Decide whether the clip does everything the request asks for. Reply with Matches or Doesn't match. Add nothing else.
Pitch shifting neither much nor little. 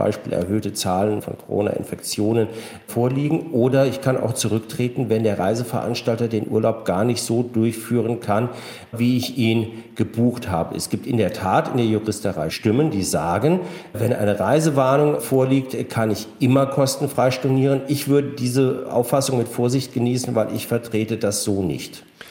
Matches